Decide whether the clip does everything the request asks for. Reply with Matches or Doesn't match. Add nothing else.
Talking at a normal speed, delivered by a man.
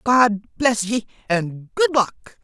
Matches